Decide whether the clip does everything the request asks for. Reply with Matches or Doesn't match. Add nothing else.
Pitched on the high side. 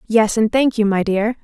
Matches